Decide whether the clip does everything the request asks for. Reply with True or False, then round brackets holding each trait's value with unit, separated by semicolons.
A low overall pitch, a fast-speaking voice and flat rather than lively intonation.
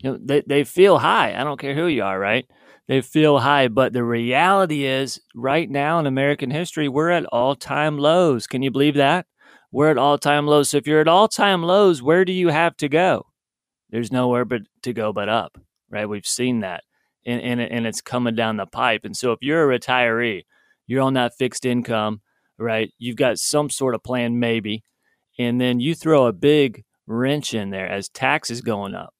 False (130 Hz; 210 wpm; 3.9 semitones)